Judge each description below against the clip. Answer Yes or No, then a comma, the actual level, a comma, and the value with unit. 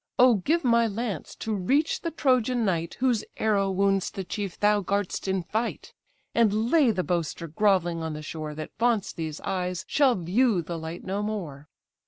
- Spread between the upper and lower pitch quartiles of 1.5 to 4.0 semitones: No, average, 5.1 semitones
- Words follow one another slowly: No, average, 180 wpm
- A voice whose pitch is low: No, high, 200 Hz